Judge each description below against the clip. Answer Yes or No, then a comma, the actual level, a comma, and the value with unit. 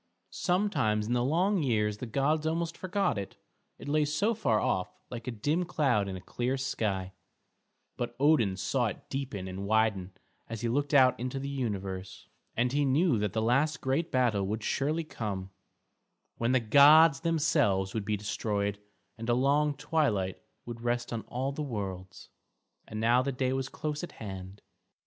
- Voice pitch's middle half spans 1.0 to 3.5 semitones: No, wide, 5.6 semitones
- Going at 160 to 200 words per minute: Yes, average, 175 wpm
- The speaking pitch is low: Yes, low, 125 Hz